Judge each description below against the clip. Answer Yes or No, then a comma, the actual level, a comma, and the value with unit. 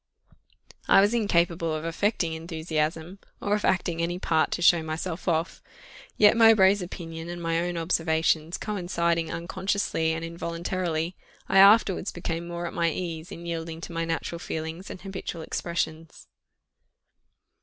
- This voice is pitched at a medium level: Yes, medium, 170 Hz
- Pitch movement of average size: No, narrow, 2.1 semitones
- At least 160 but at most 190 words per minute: No, average, 145 wpm